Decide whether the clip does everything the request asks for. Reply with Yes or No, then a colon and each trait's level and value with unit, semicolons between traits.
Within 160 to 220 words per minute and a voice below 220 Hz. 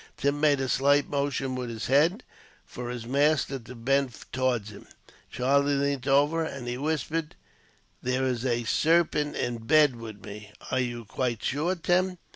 Yes: average, 170 wpm; low, 135 Hz